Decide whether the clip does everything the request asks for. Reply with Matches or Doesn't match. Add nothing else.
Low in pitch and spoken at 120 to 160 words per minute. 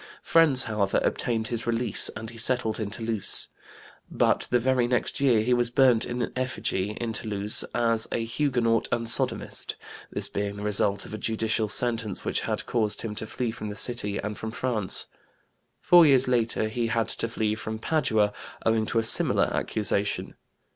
Doesn't match